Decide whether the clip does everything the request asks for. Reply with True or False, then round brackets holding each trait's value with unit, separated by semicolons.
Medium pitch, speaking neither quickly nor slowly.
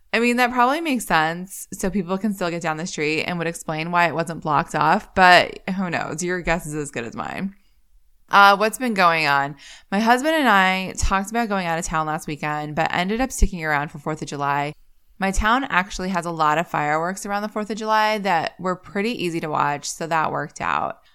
False (175 Hz; 230 wpm)